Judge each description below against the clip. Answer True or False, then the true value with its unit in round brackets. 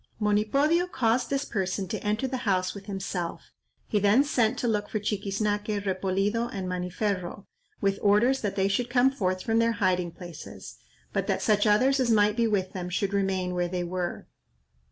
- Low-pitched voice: False (205 Hz)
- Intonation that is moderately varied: True (3.5 semitones)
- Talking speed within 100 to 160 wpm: False (180 wpm)